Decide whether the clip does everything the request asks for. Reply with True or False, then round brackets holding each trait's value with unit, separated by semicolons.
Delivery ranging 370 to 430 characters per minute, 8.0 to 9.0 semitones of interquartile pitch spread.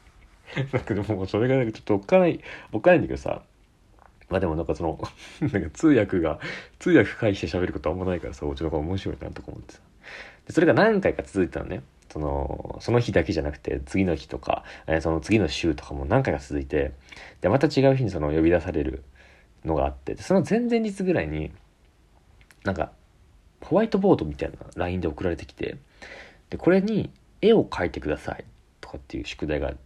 True (400 characters per minute; 8.7 semitones)